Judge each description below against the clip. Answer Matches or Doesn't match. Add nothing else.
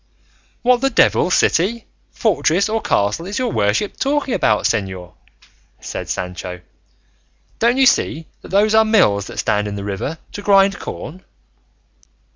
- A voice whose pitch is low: Doesn't match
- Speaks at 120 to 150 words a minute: Matches